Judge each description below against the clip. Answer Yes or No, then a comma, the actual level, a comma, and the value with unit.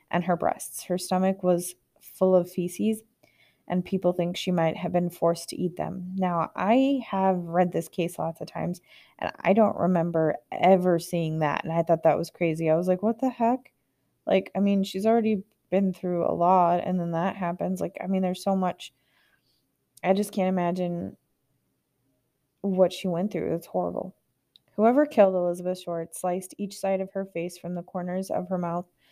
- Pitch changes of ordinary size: No, narrow, 1.9 semitones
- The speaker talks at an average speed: Yes, average, 190 wpm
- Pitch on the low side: No, medium, 180 Hz